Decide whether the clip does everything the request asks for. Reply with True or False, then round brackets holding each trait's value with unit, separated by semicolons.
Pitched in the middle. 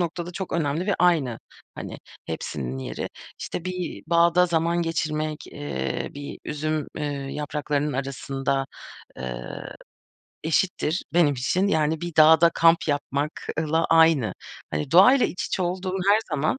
True (160 Hz)